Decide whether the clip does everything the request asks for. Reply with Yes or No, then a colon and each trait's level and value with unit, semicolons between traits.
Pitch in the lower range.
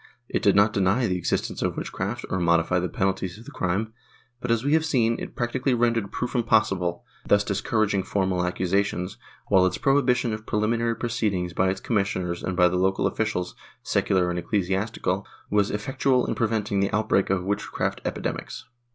Yes: low, 100 Hz